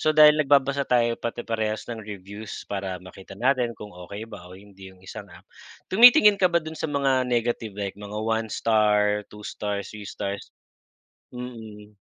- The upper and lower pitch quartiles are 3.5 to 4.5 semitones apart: Yes, average, 4.0 semitones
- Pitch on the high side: No, low, 110 Hz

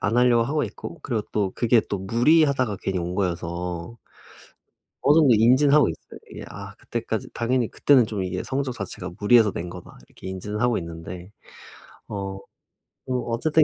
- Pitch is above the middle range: No, low, 110 Hz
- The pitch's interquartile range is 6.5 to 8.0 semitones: No, average, 5.3 semitones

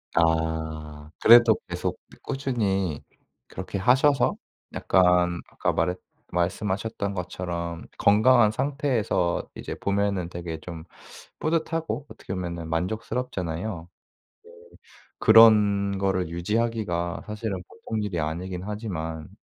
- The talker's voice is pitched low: Yes, very low, 95 Hz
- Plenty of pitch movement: No, average, 4.3 semitones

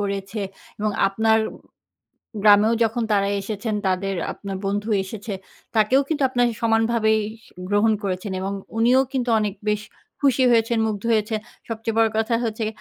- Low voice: No, high, 220 Hz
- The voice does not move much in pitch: Yes, narrow, 2.1 semitones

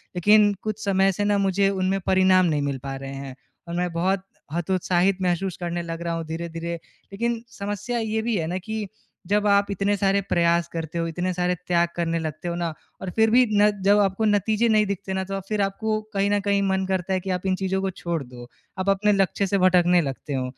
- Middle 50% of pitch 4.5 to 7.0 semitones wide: No, average, 2.8 semitones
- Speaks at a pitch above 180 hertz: Yes, high, 190 Hz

